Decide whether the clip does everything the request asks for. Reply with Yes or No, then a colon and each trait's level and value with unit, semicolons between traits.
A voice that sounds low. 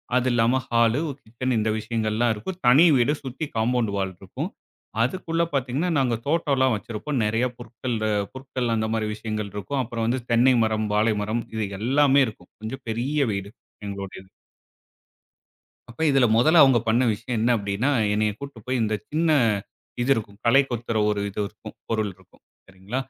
Yes: low, 115 Hz